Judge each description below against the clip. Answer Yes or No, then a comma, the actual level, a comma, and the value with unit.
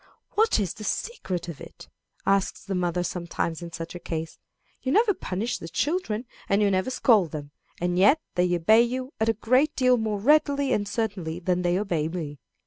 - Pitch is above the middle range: Yes, high, 195 Hz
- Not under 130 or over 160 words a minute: No, average, 190 wpm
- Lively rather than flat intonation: Yes, wide, 5.8 semitones